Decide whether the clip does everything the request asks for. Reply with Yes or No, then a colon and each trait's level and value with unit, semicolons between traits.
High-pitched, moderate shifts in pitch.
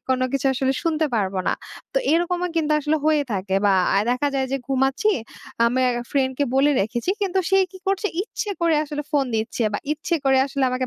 Yes: very high, 275 Hz; average, 3.9 semitones